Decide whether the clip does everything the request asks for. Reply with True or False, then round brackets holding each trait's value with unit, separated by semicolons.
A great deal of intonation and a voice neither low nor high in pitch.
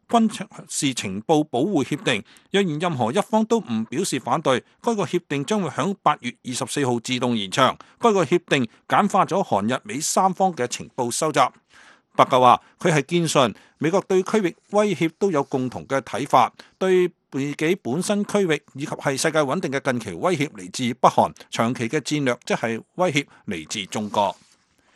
True (6.7 semitones; 155 Hz)